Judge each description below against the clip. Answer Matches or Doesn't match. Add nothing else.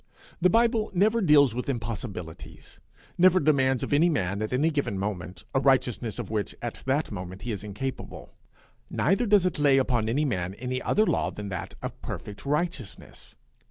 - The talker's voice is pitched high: Doesn't match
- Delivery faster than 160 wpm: Matches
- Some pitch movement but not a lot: Doesn't match